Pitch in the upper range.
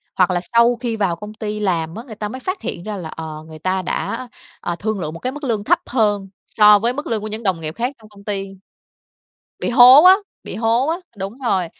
Yes: high, 210 Hz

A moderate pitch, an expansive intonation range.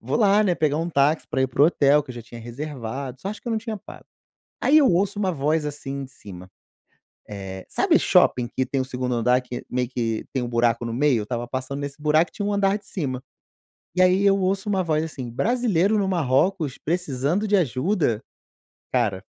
Yes: medium, 145 Hz; wide, 7.0 semitones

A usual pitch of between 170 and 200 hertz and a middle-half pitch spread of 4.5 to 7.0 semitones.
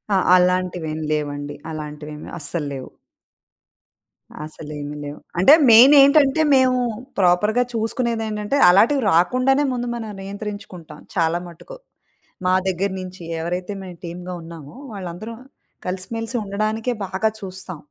Yes: medium, 185 Hz; average, 5.2 semitones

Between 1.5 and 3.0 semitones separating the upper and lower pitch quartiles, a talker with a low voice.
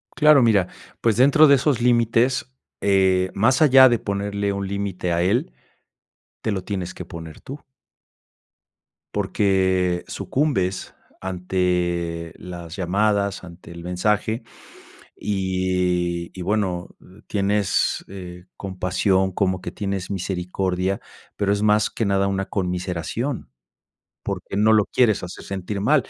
Yes: average, 2.7 semitones; very low, 95 Hz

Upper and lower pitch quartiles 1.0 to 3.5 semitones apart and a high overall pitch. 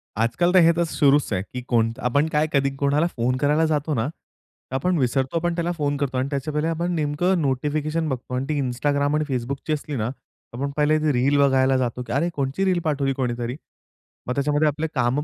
No: average, 3.0 semitones; medium, 145 Hz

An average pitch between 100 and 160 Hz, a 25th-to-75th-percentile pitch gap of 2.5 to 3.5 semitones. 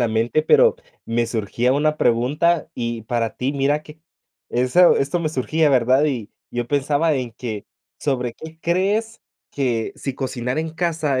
No: low, 135 Hz; average, 4.6 semitones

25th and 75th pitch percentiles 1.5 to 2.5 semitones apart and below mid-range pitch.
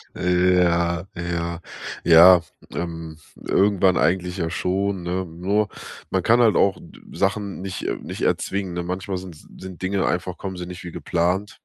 Yes: narrow, 2.0 semitones; very low, 90 Hz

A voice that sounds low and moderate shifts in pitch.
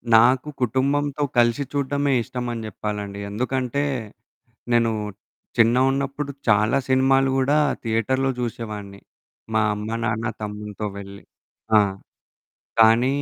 Yes: low, 120 Hz; average, 3.7 semitones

